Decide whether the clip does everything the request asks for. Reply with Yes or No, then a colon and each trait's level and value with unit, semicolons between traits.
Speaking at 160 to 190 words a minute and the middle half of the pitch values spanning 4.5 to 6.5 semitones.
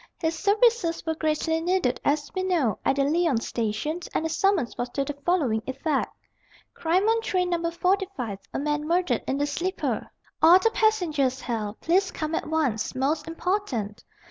Yes: average, 170 wpm; average, 5.1 semitones